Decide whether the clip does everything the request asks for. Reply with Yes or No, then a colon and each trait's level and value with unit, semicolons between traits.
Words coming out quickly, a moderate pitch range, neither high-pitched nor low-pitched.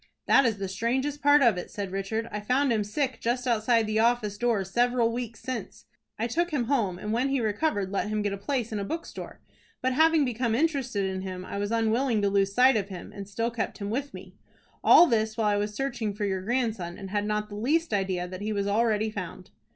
No: fast, 235 wpm; average, 3.7 semitones; high, 220 Hz